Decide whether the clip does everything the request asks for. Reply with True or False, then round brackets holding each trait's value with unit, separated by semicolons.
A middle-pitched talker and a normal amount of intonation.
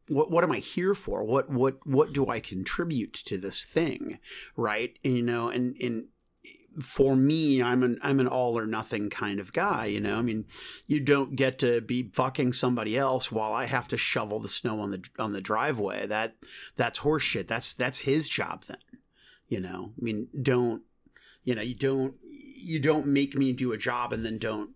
False (125 Hz; 3.5 semitones)